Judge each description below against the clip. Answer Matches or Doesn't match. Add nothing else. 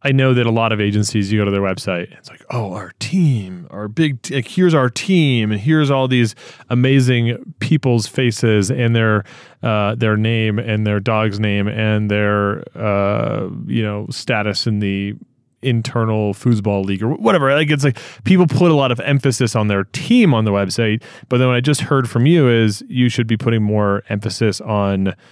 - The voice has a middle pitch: Doesn't match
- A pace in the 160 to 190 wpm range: Doesn't match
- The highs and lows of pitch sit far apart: Doesn't match